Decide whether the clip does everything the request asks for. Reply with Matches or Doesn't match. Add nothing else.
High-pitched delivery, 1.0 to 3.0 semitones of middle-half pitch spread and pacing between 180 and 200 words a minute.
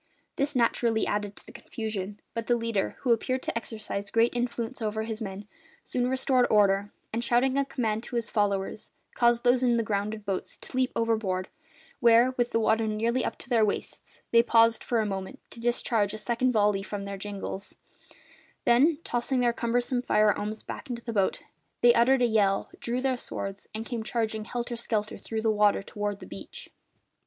Matches